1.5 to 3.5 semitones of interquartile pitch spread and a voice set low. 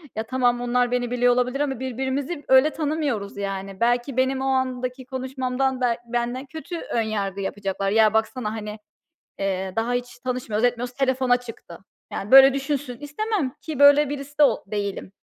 No: average, 3.2 semitones; very high, 250 Hz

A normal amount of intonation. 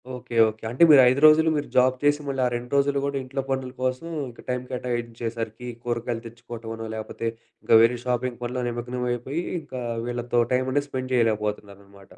No: narrow, 2.0 semitones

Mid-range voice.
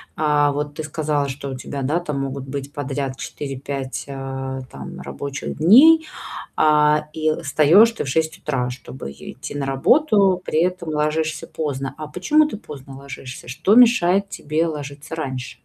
Yes: medium, 150 Hz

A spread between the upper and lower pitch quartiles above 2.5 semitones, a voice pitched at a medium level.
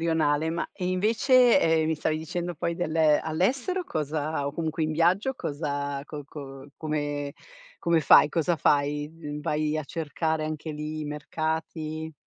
No: narrow, 2.0 semitones; medium, 155 Hz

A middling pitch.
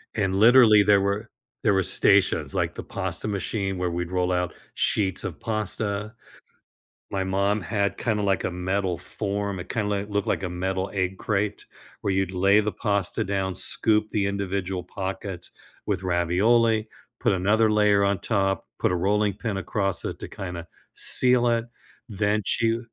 No: low, 100 Hz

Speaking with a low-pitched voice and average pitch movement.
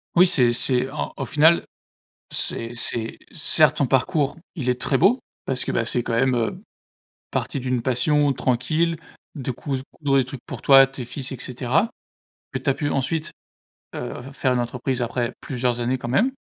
Yes: low, 130 Hz; average, 3.1 semitones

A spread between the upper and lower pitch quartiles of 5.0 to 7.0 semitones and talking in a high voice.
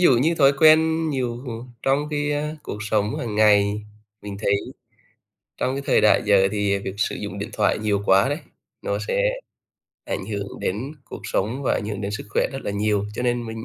No: wide, 5.5 semitones; low, 110 Hz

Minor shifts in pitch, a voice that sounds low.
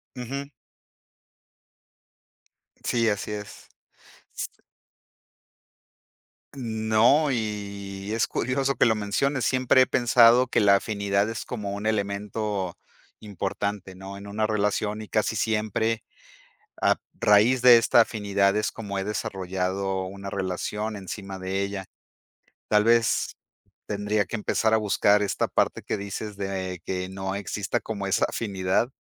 Yes: narrow, 2.1 semitones; low, 105 Hz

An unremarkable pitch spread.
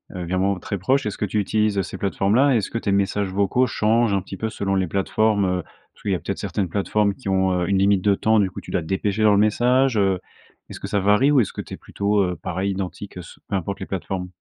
No: narrow, 2.1 semitones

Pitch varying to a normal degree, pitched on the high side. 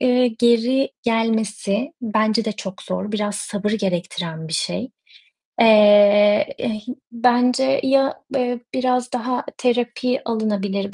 Yes: average, 3.2 semitones; high, 225 Hz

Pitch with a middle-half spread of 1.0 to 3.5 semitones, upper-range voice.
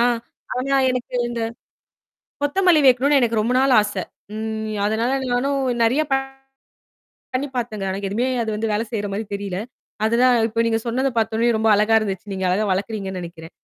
Yes: average, 3.2 semitones; high, 225 Hz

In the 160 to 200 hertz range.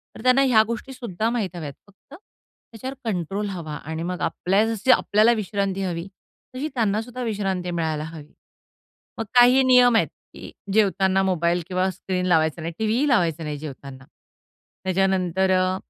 Yes: high, 190 Hz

